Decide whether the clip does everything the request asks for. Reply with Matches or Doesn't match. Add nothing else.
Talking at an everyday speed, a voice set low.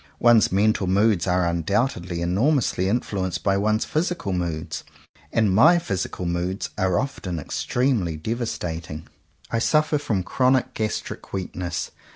Doesn't match